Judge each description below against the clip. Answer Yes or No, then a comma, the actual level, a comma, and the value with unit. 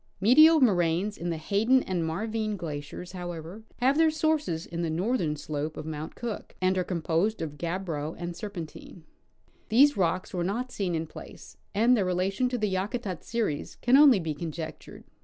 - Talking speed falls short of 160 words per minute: No, average, 175 wpm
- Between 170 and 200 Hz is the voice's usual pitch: Yes, medium, 185 Hz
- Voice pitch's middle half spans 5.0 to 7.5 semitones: Yes, wide, 5.5 semitones